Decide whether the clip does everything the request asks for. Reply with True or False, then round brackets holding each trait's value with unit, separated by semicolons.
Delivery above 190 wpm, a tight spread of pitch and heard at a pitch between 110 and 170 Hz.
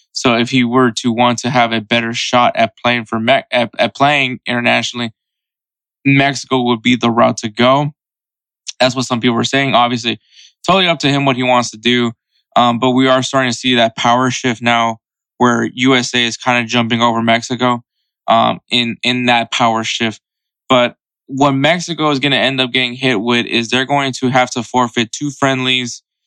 True (200 wpm; 1.7 semitones; 125 Hz)